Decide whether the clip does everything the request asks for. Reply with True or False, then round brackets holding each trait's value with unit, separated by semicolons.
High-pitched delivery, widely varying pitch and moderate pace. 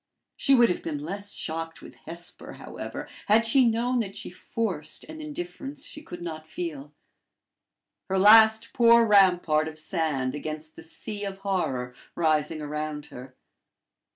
False (175 Hz; 6.4 semitones; 150 wpm)